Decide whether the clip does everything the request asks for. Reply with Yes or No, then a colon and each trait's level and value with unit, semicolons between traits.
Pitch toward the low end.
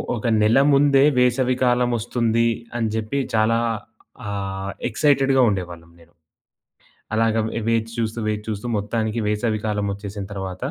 Yes: low, 110 Hz